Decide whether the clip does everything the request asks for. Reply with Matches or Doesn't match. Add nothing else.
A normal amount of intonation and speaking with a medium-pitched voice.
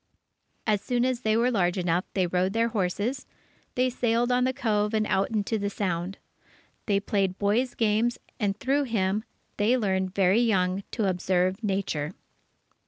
Doesn't match